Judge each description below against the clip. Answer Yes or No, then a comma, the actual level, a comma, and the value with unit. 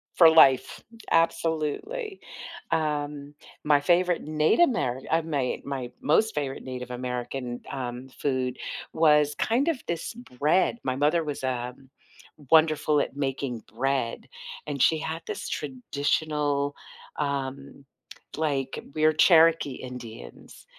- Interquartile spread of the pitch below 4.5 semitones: Yes, average, 3.3 semitones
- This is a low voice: No, medium, 145 Hz